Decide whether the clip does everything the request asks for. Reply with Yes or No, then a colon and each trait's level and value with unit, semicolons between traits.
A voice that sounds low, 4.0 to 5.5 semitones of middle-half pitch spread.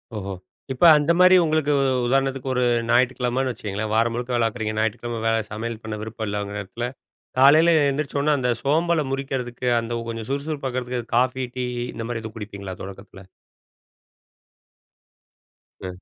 No: low, 120 Hz; average, 3.5 semitones